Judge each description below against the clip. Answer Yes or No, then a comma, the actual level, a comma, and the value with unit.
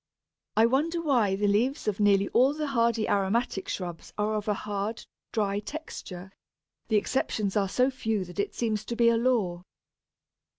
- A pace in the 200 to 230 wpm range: No, average, 170 wpm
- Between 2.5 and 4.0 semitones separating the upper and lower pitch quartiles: Yes, average, 3.3 semitones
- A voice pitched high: Yes, high, 215 Hz